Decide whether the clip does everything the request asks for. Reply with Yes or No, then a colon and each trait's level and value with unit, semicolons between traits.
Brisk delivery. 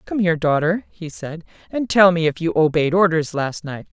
Yes: fast, 210 wpm